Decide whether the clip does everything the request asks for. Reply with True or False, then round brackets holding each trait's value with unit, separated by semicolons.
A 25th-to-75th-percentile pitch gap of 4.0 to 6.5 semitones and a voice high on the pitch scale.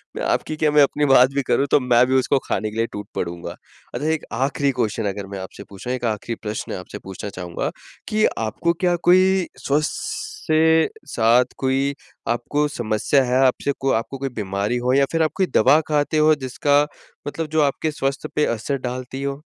False (4.7 semitones; 135 Hz)